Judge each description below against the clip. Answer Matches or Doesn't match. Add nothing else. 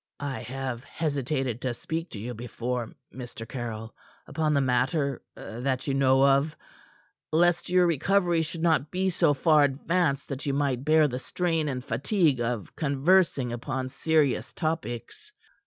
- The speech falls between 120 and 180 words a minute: Matches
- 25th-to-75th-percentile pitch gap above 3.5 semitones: Matches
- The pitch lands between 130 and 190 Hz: Matches